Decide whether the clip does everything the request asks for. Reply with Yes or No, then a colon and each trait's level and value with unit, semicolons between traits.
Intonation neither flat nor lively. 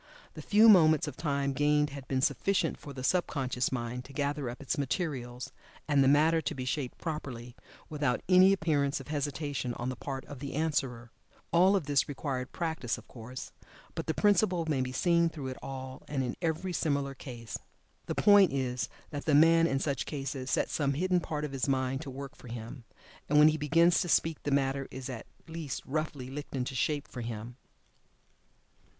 Yes: average, 3.4 semitones